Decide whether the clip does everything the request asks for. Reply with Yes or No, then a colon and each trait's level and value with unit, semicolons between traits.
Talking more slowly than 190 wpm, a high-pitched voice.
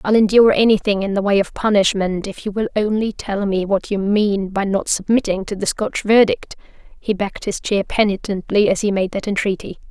No: fast, 205 wpm; high, 200 Hz